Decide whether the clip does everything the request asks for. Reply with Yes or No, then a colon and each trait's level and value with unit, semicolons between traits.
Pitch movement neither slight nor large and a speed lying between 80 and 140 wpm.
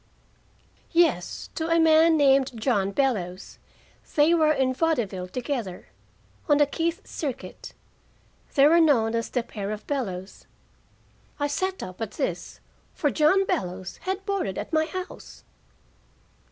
No: wide, 7.2 semitones; slow, 135 wpm